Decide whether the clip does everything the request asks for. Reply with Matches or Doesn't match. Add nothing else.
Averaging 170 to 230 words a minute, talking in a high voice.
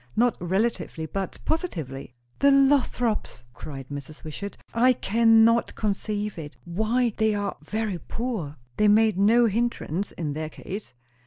Doesn't match